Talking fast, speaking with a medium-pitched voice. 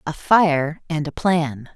No: average, 170 wpm; medium, 155 Hz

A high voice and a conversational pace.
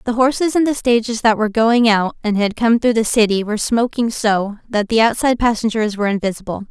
No: high, 225 Hz; fast, 215 wpm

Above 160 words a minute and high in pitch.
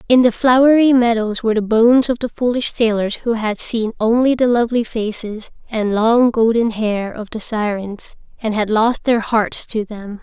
Yes: average, 190 wpm; high, 225 Hz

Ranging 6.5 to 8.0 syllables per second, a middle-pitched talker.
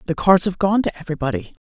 Yes: 7.4 syllables/s; medium, 175 Hz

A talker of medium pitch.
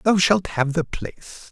Yes: medium, 175 Hz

